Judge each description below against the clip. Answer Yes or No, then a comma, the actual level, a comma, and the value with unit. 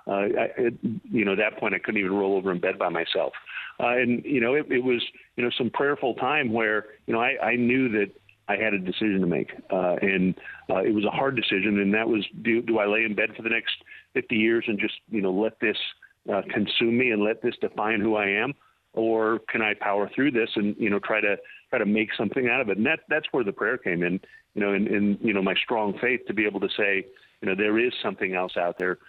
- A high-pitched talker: No, low, 105 Hz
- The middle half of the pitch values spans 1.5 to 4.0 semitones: Yes, narrow, 2.4 semitones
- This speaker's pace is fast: Yes, fast, 265 wpm